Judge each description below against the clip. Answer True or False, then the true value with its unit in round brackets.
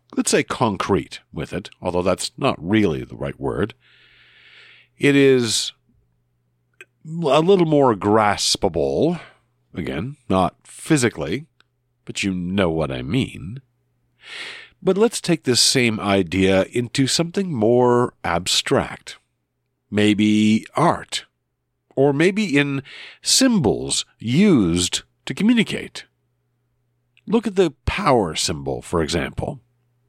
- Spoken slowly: True (105 wpm)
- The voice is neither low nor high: False (120 Hz)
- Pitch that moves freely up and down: True (8.3 semitones)